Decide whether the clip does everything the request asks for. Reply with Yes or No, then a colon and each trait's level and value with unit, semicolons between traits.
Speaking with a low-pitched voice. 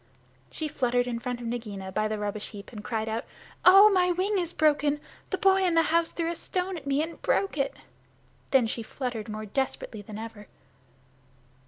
No: very high, 260 Hz